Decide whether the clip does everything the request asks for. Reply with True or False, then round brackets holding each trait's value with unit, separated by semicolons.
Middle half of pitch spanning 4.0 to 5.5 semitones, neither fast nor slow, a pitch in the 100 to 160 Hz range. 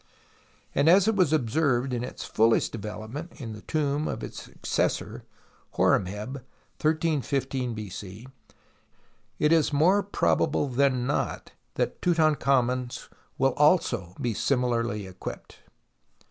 False (4.9 semitones; 110 wpm; 135 Hz)